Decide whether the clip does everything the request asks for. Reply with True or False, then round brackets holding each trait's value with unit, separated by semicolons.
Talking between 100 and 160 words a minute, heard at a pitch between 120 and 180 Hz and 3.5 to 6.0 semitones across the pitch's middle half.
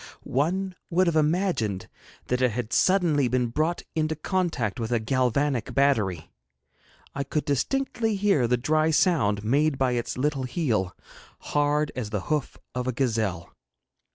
True (150 wpm; 140 Hz; 4.9 semitones)